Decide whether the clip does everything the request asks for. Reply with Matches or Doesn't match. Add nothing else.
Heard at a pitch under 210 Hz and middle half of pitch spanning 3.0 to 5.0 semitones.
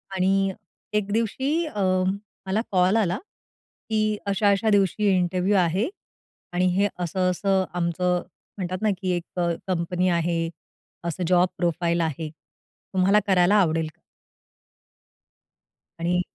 Doesn't match